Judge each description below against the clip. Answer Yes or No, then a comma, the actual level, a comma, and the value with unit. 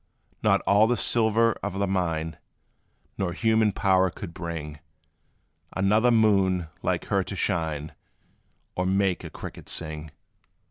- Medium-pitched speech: No, very low, 95 Hz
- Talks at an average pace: No, slow, 130 wpm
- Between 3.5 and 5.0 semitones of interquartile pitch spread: Yes, average, 3.8 semitones